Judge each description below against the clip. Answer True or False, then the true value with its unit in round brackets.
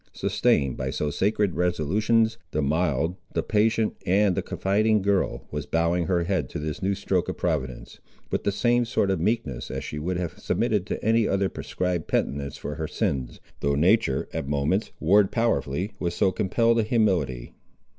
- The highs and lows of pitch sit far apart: True (5.9 semitones)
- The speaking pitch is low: True (90 Hz)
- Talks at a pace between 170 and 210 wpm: True (175 wpm)